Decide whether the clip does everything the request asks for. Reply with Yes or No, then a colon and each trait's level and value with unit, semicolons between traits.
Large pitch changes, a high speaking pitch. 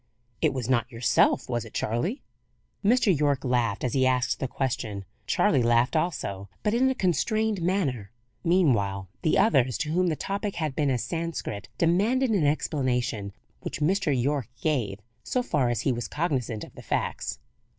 No: wide, 6.6 semitones; low, 135 Hz